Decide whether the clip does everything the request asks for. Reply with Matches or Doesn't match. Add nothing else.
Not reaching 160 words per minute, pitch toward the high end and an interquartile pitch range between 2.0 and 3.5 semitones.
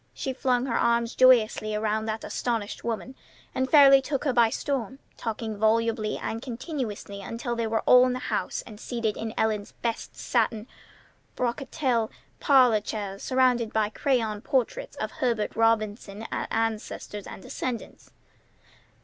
Matches